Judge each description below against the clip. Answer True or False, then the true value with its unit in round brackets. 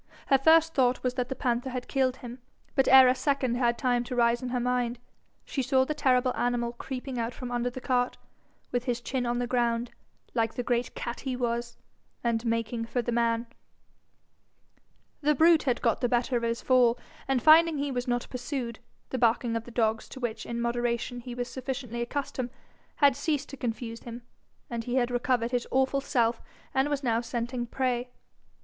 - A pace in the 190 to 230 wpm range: True (195 wpm)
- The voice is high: True (245 Hz)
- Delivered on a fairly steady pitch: True (1.7 semitones)